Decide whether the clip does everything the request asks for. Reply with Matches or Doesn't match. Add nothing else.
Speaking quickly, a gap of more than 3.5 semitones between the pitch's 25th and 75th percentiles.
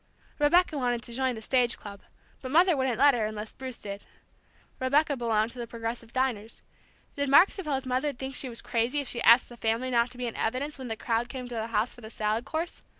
Doesn't match